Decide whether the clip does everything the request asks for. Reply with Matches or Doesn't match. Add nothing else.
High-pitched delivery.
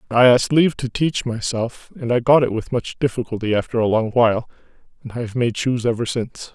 Doesn't match